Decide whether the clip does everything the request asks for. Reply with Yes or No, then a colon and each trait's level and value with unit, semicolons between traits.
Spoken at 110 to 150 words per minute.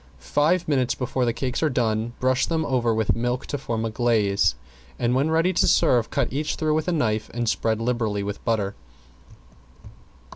No: average, 185 wpm